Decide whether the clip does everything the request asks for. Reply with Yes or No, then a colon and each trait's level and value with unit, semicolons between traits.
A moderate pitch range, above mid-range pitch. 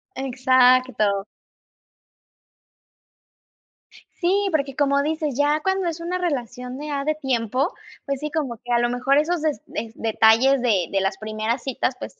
Yes: average, 4.0 semitones; very high, 270 Hz